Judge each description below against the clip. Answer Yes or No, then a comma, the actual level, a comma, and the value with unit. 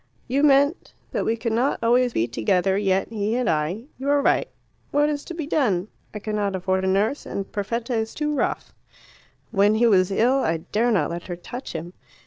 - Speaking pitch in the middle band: No, high, 220 Hz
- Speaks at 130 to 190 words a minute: No, fast, 205 wpm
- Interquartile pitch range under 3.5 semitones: No, average, 5.1 semitones